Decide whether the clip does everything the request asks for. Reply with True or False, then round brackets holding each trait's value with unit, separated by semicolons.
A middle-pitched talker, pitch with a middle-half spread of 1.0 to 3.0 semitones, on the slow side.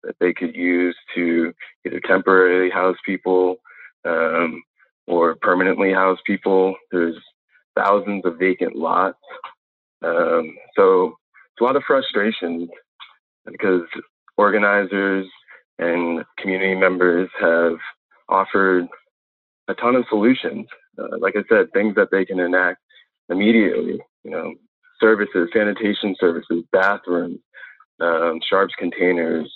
False (95 Hz; 2.7 semitones; 115 wpm)